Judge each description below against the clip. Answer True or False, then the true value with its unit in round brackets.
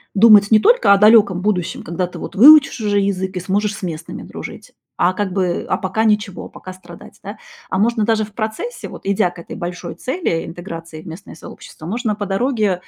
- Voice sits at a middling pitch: False (200 Hz)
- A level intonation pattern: False (3.2 semitones)